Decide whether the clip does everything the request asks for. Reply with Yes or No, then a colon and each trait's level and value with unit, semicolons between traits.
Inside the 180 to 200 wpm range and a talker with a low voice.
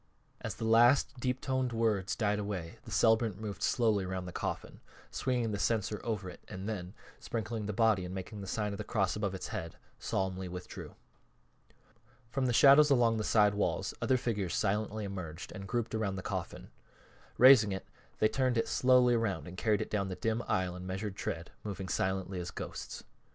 Yes: average, 190 wpm; low, 105 Hz